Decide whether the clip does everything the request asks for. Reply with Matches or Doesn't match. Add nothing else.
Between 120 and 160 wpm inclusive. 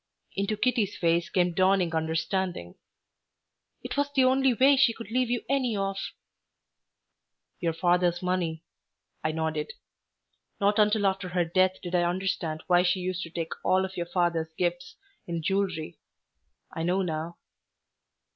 Matches